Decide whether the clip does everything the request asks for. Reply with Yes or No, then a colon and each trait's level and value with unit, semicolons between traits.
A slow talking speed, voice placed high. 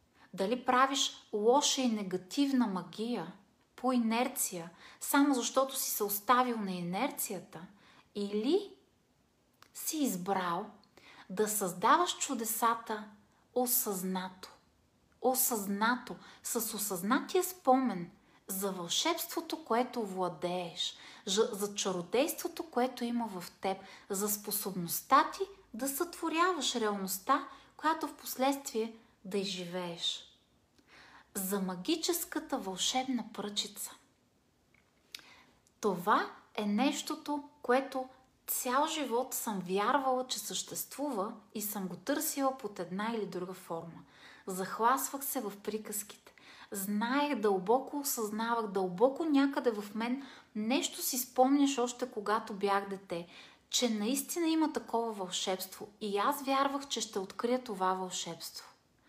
Yes: slow, 105 wpm; high, 230 Hz